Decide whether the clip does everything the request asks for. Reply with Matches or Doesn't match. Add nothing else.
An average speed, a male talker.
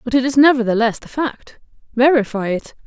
Doesn't match